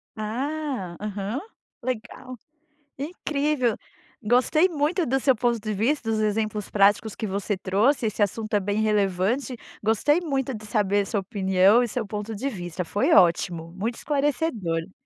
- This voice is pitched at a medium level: No, high, 215 Hz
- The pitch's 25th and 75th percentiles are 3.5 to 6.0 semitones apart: Yes, average, 4.7 semitones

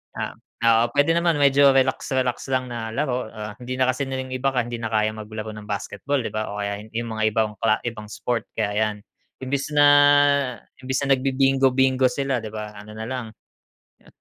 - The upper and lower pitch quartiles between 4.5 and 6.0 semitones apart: No, average, 3.5 semitones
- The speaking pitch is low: Yes, low, 125 Hz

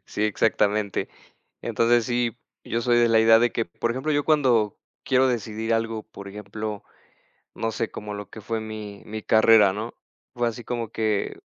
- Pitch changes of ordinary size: No, narrow, 1.9 semitones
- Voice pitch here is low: Yes, low, 110 Hz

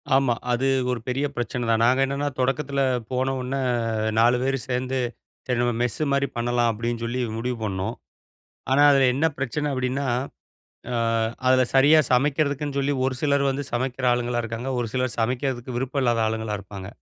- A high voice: No, low, 130 Hz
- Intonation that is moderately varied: No, narrow, 2.2 semitones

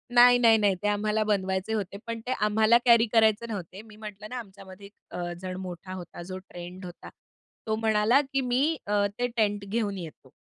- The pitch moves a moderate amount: Yes, average, 3.0 semitones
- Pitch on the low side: No, high, 210 Hz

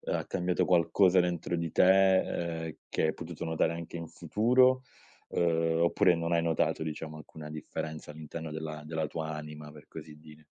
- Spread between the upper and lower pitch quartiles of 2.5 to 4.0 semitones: No, narrow, 2.0 semitones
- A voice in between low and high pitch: No, very low, 80 Hz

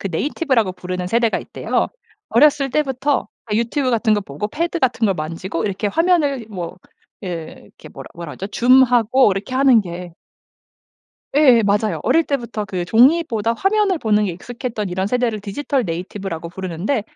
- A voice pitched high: Yes, high, 225 Hz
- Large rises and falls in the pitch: Yes, wide, 5.9 semitones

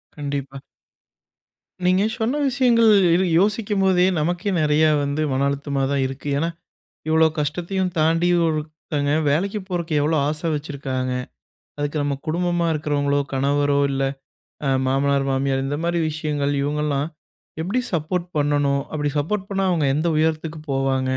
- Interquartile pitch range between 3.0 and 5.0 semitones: Yes, average, 3.4 semitones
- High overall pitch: No, medium, 150 Hz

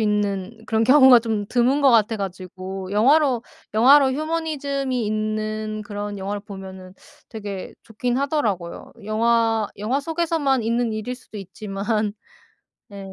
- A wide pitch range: No, average, 4.1 semitones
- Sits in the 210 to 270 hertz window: Yes, high, 220 Hz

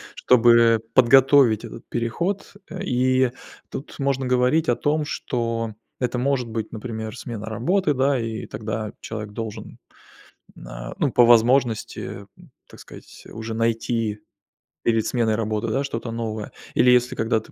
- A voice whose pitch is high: No, low, 115 Hz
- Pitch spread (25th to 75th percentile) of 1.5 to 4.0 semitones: Yes, average, 2.7 semitones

